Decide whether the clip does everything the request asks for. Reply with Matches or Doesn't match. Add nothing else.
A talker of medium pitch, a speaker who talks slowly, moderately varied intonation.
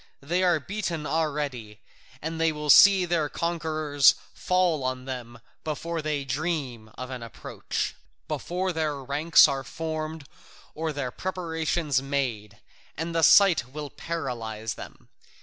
Matches